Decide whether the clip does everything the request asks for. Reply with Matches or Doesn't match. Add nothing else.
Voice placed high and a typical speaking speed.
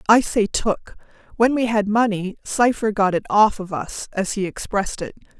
Matches